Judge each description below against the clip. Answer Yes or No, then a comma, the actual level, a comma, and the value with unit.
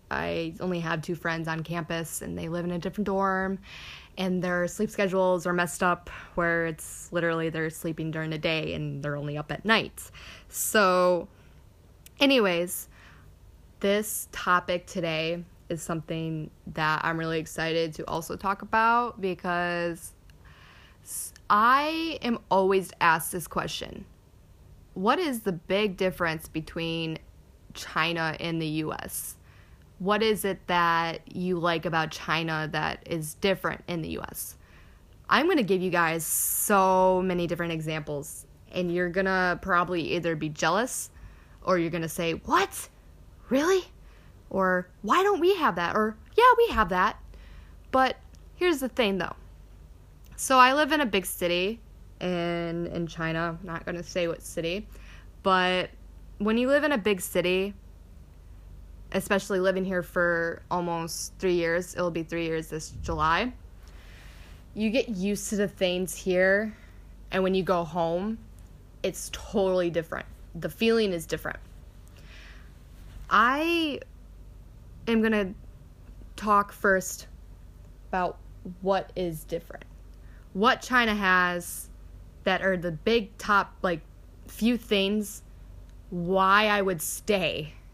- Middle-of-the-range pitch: Yes, medium, 175 Hz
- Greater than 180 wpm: No, slow, 135 wpm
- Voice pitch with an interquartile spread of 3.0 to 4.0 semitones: Yes, average, 3.5 semitones